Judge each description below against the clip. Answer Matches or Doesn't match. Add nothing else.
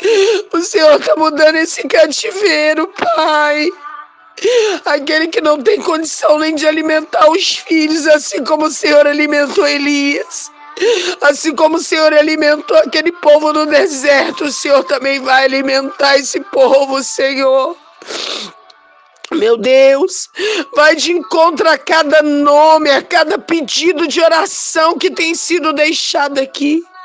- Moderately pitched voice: Doesn't match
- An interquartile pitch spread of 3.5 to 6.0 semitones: Doesn't match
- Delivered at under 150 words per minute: Matches